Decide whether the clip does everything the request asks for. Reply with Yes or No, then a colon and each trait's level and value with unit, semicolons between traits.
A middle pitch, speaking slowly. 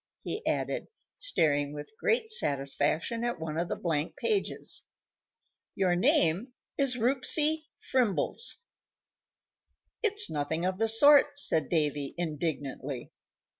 Yes: medium, 180 Hz; slow, 110 wpm